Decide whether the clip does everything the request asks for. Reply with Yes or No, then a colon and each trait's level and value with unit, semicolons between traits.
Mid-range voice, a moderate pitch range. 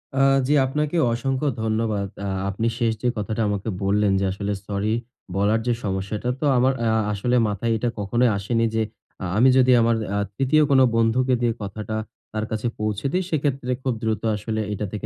No: low, 110 Hz; average, 3.4 semitones